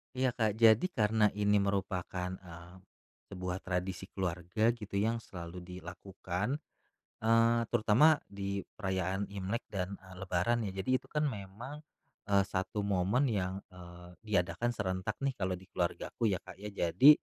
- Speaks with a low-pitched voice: Yes, low, 100 Hz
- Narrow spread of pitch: No, average, 3.3 semitones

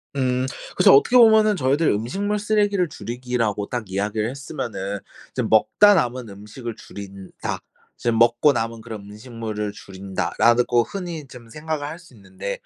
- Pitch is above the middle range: No, low, 120 Hz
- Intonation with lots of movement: Yes, wide, 6.2 semitones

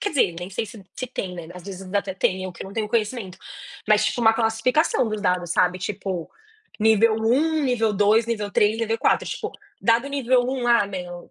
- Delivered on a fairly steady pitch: No, average, 3.8 semitones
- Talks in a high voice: Yes, high, 215 Hz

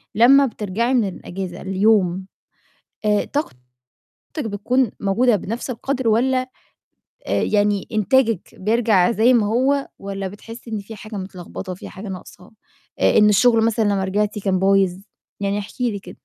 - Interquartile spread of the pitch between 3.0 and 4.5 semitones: Yes, average, 3.3 semitones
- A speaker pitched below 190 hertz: No, high, 210 Hz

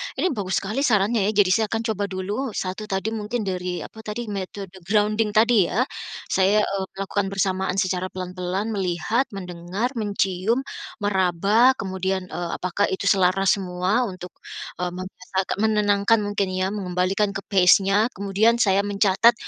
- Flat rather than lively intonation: Yes, narrow, 2.2 semitones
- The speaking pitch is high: Yes, high, 195 Hz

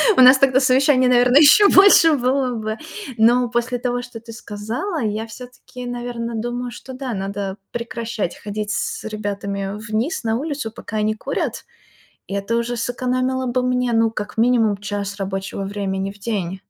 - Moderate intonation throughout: Yes, average, 3.3 semitones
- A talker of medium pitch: No, high, 235 Hz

